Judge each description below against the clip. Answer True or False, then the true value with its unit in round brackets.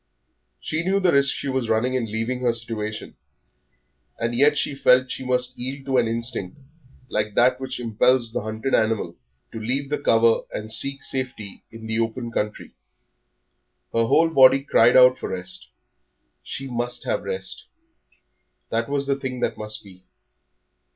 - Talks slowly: False (165 wpm)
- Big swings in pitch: False (3.1 semitones)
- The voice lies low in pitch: True (125 Hz)